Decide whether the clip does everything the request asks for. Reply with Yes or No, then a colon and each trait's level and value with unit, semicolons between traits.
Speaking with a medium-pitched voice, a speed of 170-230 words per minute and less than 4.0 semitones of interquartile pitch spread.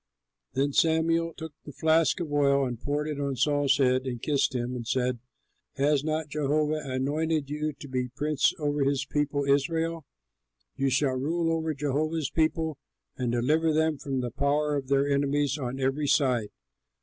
Yes: medium, 145 Hz; average, 175 wpm; narrow, 2.5 semitones